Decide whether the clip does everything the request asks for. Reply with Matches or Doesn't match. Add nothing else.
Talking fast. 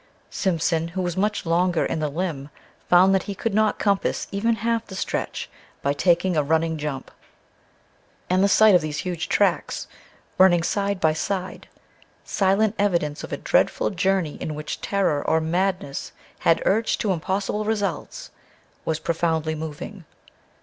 Doesn't match